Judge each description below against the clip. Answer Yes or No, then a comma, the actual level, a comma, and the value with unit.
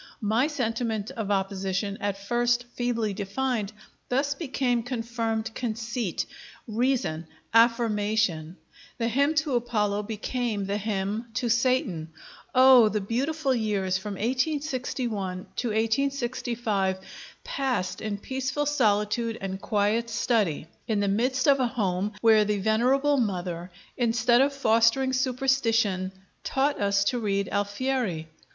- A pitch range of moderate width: Yes, average, 3.9 semitones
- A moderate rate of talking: No, slow, 120 wpm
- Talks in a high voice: Yes, high, 225 Hz